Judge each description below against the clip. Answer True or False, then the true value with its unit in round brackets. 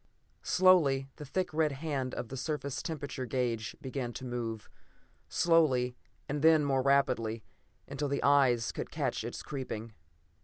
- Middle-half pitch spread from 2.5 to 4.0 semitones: True (3.2 semitones)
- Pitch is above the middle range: False (135 Hz)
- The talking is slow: False (145 wpm)